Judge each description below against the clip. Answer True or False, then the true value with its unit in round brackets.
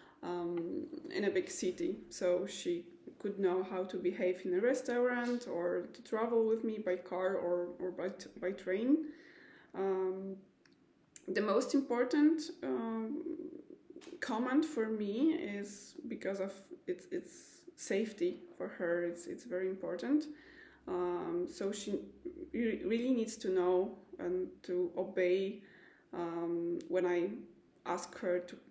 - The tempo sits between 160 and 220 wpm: False (135 wpm)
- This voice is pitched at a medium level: False (225 Hz)